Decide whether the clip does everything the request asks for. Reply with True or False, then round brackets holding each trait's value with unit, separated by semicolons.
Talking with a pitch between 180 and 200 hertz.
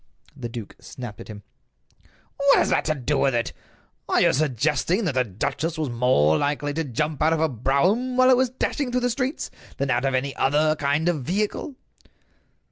False (150 Hz)